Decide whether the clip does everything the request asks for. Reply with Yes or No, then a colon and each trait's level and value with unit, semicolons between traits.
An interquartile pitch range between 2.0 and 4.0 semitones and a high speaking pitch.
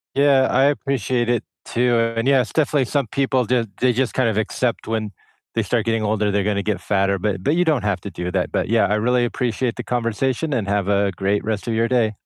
No: average, 3.7 semitones; low, 115 Hz